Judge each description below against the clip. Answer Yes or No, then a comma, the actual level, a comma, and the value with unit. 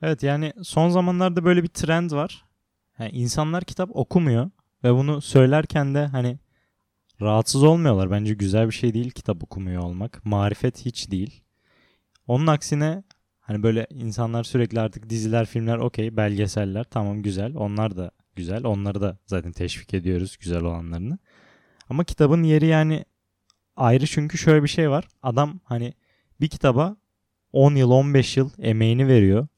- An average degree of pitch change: No, wide, 6.3 semitones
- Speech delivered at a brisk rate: Yes, fast, 150 wpm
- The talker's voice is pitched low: Yes, low, 120 Hz